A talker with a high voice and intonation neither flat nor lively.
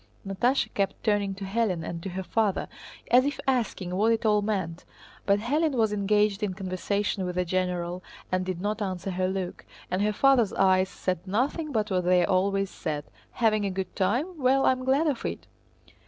Yes: high, 200 Hz; average, 3.4 semitones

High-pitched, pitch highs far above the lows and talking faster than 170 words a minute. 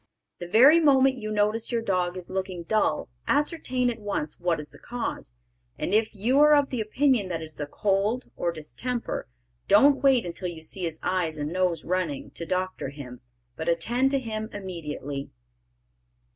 Yes: high, 195 Hz; wide, 6.5 semitones; average, 180 wpm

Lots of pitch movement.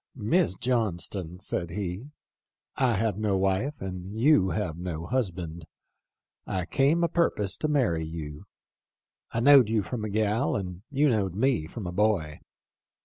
Yes: wide, 5.9 semitones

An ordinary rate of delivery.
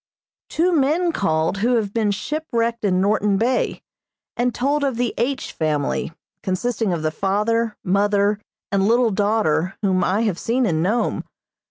Yes: average, 155 wpm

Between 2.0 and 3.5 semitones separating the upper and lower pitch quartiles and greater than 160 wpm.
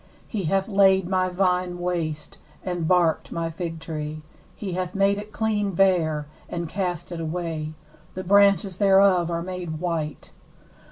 No: average, 2.7 semitones; average, 150 wpm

